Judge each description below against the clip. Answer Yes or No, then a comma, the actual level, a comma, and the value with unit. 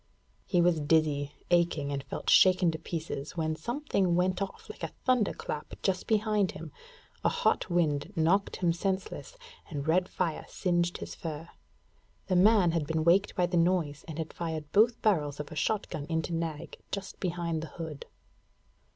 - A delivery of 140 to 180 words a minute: Yes, average, 170 wpm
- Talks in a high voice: No, medium, 170 Hz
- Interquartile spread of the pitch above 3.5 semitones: No, average, 2.9 semitones